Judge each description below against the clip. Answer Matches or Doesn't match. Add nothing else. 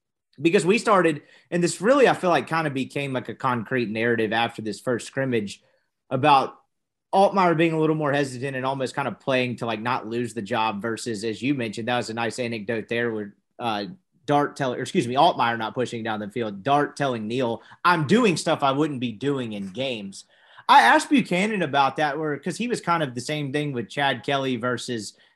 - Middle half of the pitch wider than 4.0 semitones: Matches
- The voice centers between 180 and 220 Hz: Doesn't match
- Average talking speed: Doesn't match